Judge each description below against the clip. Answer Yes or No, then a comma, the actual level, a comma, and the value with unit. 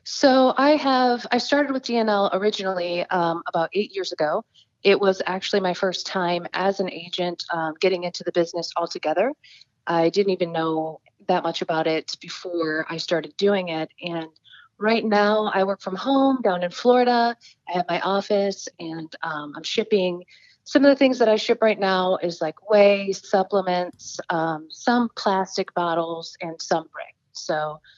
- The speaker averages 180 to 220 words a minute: No, average, 170 wpm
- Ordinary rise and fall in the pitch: Yes, average, 4.0 semitones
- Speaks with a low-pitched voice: No, medium, 185 Hz